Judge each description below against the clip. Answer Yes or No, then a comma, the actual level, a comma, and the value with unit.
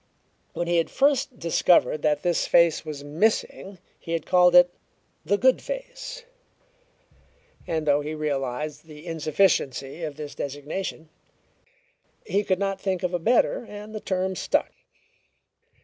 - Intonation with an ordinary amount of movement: Yes, average, 4.5 semitones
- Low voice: No, medium, 170 Hz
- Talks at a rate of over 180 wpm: No, average, 140 wpm